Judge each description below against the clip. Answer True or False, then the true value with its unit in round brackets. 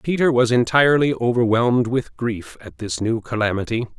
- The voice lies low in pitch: True (120 Hz)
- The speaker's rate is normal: True (150 wpm)